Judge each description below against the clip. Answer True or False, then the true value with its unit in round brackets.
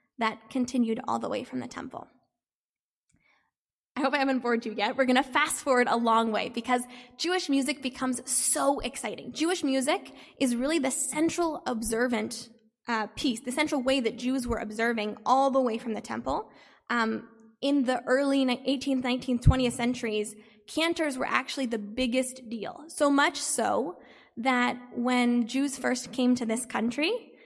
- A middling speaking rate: True (165 wpm)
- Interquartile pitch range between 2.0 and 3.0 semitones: True (2.7 semitones)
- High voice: True (255 Hz)